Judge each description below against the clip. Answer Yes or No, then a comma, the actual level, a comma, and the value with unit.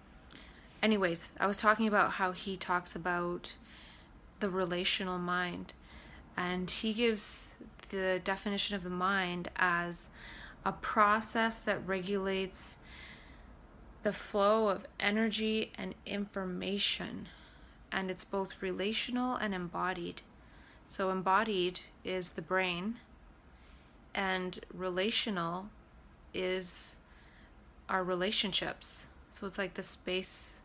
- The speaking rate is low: Yes, slow, 100 wpm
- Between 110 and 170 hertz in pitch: No, high, 190 Hz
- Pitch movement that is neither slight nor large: No, narrow, 2.3 semitones